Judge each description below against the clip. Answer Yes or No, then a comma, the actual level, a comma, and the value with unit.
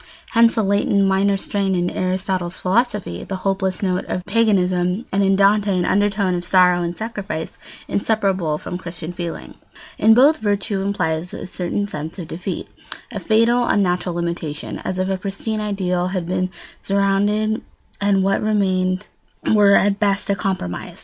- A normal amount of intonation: No, narrow, 2.2 semitones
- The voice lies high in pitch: Yes, high, 195 Hz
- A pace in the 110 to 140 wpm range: No, average, 155 wpm